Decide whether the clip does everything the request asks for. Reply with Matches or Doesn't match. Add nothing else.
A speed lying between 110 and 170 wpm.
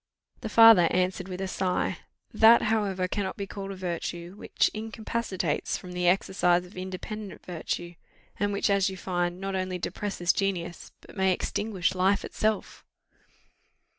Matches